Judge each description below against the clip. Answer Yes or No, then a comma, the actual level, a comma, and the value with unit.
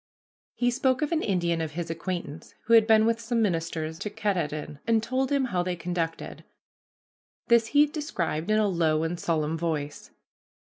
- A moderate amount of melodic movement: No, wide, 5.8 semitones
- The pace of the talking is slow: No, average, 180 wpm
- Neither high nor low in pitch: Yes, medium, 180 Hz